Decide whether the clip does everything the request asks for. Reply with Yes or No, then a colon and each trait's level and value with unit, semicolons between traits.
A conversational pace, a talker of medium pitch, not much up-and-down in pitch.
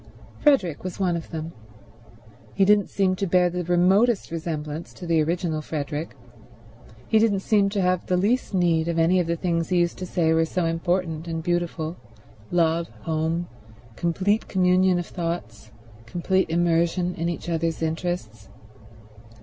Yes: average, 155 wpm; medium, 175 Hz; narrow, 2.1 semitones